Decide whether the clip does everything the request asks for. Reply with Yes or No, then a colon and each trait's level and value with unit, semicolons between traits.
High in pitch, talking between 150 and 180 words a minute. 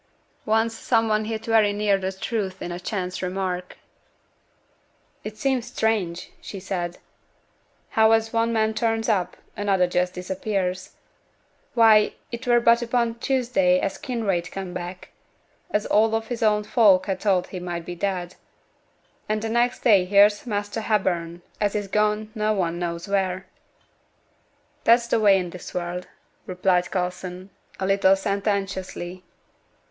No: high, 200 Hz; average, 140 wpm